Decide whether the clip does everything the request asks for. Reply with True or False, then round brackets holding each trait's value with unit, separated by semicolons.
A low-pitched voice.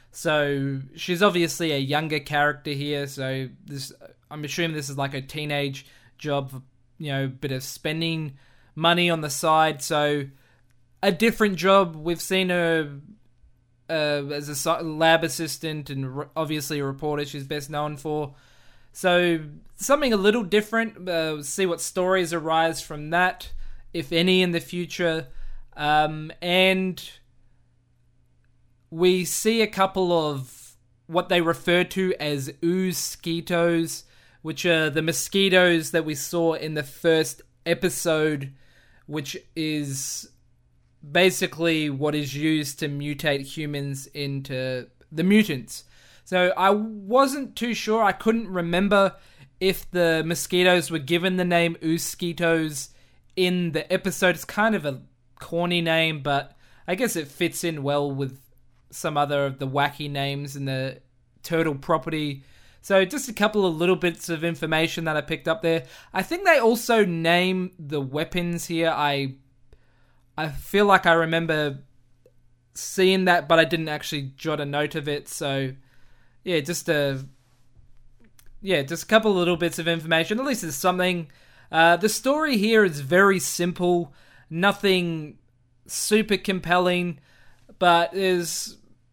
False (160 Hz)